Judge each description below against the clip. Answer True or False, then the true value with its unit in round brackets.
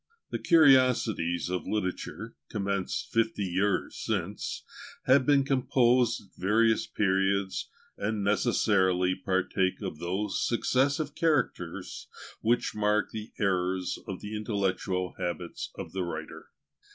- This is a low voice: True (100 Hz)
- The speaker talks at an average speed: False (115 wpm)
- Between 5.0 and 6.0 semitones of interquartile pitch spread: False (4.1 semitones)